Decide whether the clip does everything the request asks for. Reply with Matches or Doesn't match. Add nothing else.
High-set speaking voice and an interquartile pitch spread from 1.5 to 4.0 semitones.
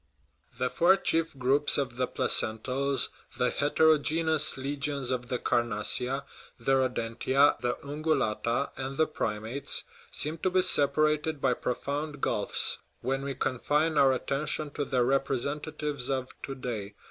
Doesn't match